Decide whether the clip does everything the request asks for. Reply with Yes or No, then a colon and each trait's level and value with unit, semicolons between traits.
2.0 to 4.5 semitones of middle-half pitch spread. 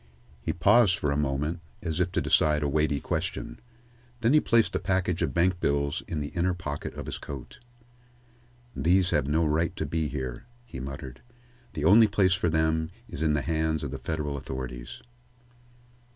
Yes: average, 3.6 semitones